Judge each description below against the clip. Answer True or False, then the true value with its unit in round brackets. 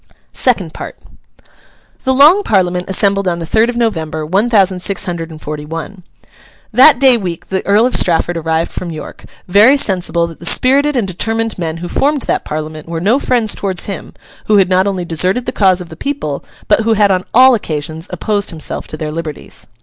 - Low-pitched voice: False (190 Hz)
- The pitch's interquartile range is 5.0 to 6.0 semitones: True (5.3 semitones)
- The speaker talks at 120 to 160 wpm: False (200 wpm)